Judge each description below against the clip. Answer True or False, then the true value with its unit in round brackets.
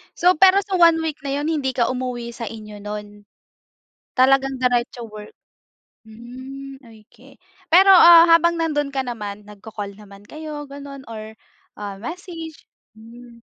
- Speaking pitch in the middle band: False (255 Hz)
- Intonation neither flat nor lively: False (5.9 semitones)